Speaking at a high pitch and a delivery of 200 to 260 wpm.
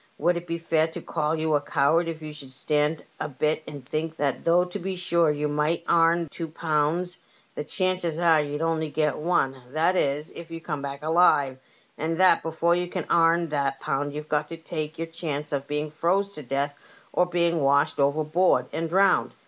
No: medium, 160 Hz; fast, 205 wpm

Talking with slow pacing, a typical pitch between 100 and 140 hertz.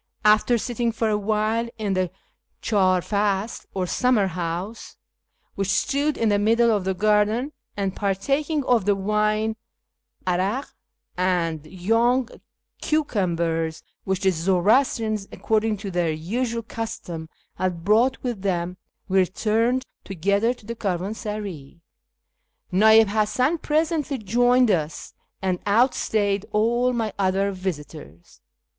No: slow, 120 wpm; high, 210 Hz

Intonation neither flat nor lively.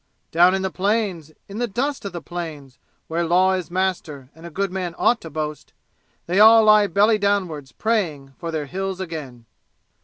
Yes: average, 4.0 semitones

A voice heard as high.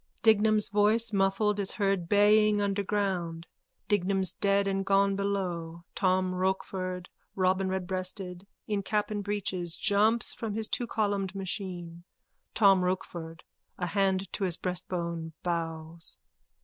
Yes: high, 195 Hz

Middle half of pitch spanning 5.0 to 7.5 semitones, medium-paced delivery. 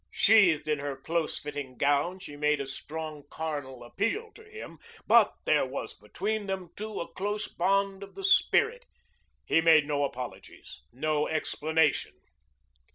Yes: wide, 5.4 semitones; average, 150 wpm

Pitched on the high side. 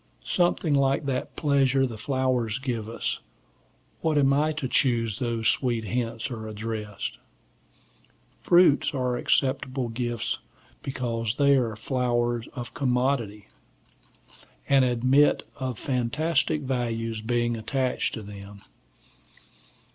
No: low, 125 Hz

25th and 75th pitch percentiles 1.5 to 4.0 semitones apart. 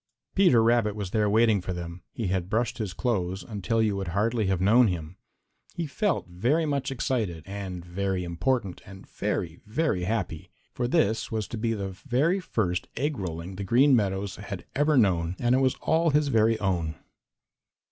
No: average, 5.1 semitones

